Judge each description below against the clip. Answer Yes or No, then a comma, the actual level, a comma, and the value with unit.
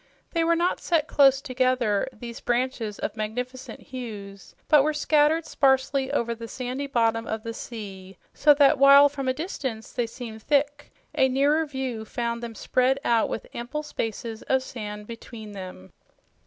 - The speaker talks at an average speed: Yes, average, 165 wpm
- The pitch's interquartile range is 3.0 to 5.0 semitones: Yes, average, 3.7 semitones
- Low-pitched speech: No, very high, 255 Hz